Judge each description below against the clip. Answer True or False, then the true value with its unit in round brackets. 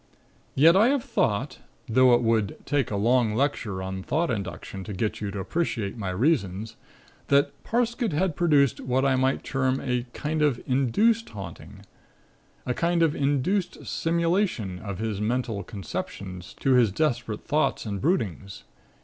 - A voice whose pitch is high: False (125 Hz)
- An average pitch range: False (6.7 semitones)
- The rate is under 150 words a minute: False (155 wpm)